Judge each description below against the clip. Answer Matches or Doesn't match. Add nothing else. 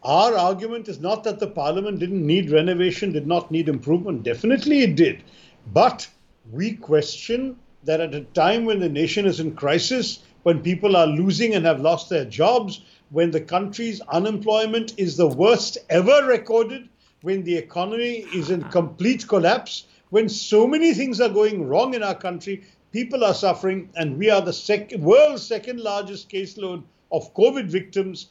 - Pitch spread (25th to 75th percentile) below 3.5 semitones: Doesn't match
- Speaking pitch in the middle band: Doesn't match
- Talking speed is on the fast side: Doesn't match